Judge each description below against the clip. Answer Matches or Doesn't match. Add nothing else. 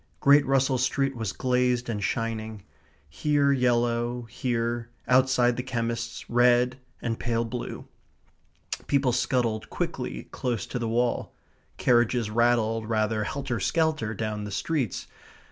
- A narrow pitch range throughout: Matches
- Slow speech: Matches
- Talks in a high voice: Doesn't match